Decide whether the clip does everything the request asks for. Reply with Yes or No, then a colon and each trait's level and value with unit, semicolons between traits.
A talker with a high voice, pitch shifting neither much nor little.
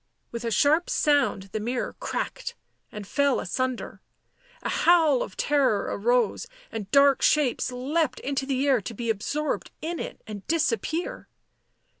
Yes: very high, 270 Hz; average, 4.7 semitones